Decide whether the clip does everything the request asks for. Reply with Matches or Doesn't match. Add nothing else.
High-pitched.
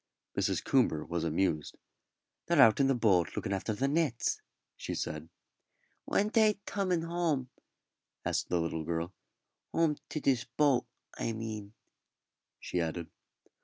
Doesn't match